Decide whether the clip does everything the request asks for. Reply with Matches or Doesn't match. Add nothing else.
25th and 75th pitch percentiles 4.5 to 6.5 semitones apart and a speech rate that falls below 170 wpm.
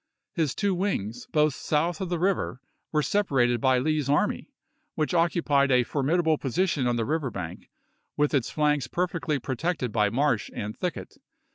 Matches